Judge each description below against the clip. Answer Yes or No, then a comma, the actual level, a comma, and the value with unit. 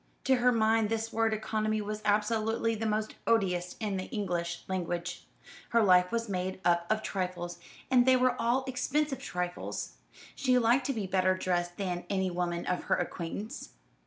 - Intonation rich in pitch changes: No, average, 4.1 semitones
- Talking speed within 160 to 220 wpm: Yes, average, 170 wpm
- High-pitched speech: Yes, high, 210 Hz